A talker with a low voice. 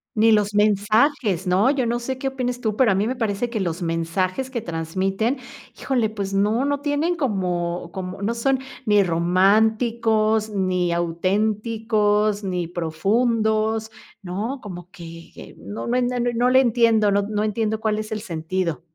No: high, 210 Hz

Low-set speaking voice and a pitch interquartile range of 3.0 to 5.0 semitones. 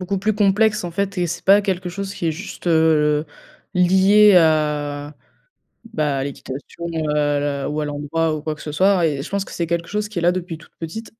No: medium, 170 Hz; average, 4.6 semitones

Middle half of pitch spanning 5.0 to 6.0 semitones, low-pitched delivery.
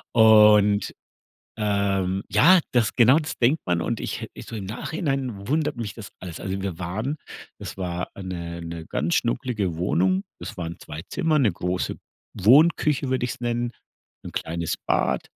Yes: average, 5.3 semitones; low, 105 Hz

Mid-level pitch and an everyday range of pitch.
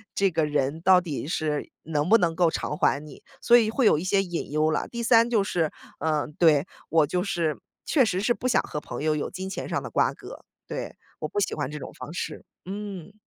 Yes: medium, 170 Hz; average, 4.8 semitones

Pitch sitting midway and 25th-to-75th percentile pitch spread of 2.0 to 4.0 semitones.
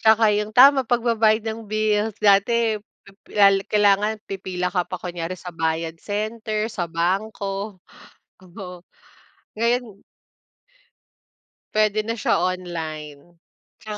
No: high, 205 Hz; average, 3.4 semitones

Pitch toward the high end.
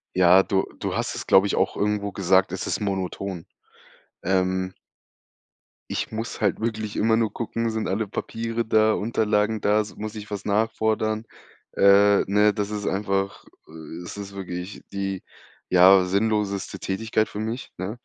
No: low, 100 Hz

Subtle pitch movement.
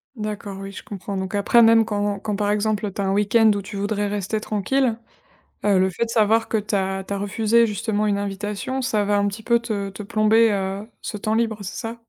Yes: narrow, 1.8 semitones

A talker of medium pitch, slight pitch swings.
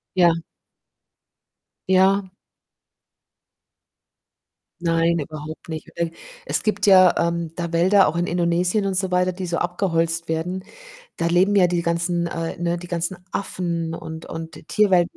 Yes: medium, 175 Hz; narrow, 1.7 semitones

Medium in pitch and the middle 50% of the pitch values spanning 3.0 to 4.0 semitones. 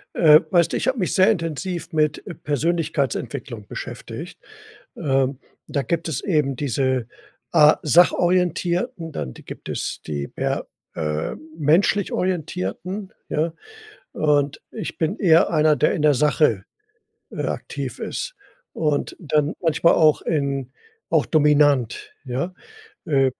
Yes: medium, 150 Hz; average, 3.7 semitones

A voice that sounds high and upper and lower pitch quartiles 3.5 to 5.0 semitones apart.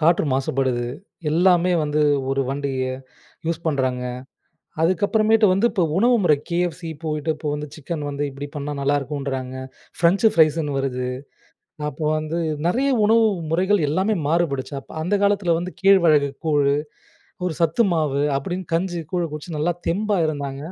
No: medium, 160 Hz; average, 4.2 semitones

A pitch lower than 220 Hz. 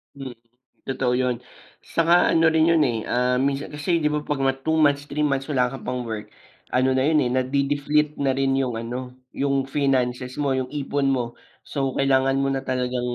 Yes: low, 135 Hz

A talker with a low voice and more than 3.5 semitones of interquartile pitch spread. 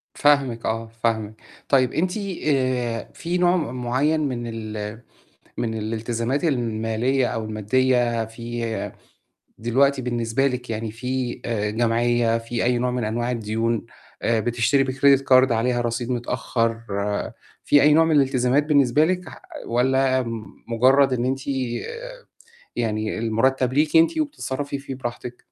No: low, 120 Hz; average, 2.8 semitones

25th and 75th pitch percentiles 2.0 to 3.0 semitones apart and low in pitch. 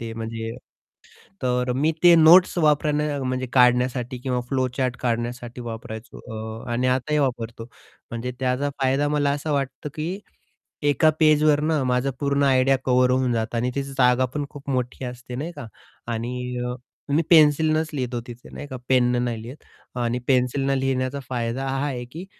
Yes: average, 2.7 semitones; low, 130 Hz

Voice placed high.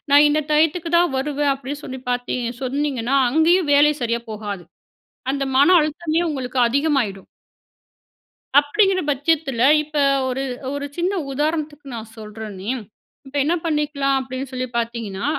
Yes: very high, 280 Hz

